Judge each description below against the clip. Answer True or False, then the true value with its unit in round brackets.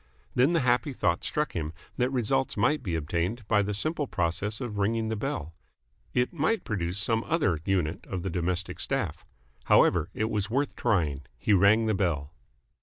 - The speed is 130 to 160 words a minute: False (180 wpm)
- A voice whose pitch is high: False (105 Hz)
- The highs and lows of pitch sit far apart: True (6.0 semitones)